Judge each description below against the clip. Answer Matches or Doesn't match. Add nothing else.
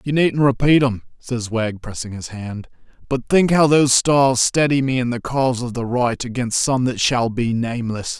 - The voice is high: Doesn't match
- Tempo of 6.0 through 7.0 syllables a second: Doesn't match